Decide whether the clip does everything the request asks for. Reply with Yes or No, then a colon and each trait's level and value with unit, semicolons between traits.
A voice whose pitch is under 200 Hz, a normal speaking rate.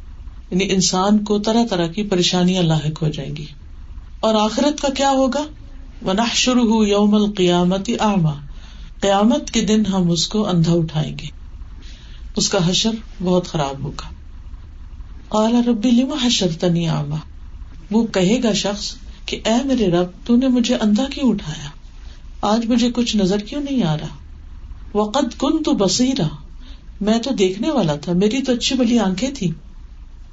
Yes: high, 190 Hz; average, 145 wpm